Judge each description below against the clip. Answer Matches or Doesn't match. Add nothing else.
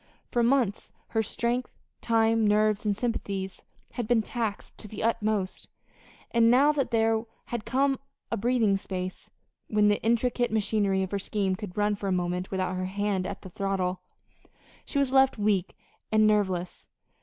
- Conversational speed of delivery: Matches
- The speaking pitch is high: Matches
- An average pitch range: Matches